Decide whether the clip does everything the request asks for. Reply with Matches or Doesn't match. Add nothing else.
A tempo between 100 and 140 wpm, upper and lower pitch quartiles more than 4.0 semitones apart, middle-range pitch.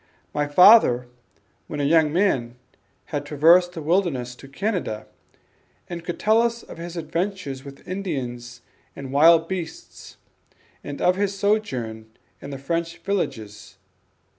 Matches